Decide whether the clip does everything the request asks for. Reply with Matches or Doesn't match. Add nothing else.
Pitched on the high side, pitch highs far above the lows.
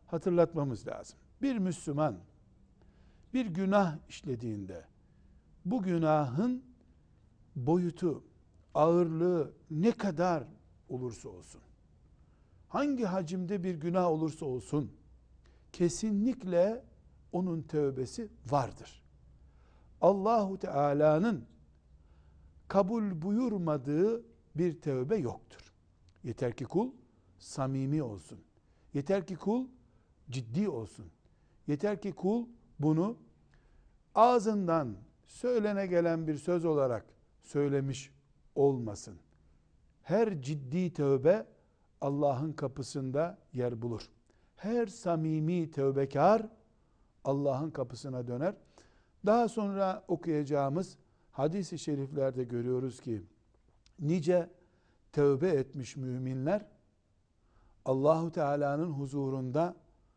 Doesn't match